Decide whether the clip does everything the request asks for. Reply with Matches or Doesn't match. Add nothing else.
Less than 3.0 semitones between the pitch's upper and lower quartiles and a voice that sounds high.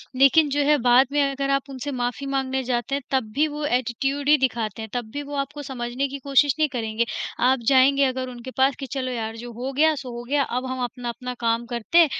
Matches